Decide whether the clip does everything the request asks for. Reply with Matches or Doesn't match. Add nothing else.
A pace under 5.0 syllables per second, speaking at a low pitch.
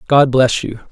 Matches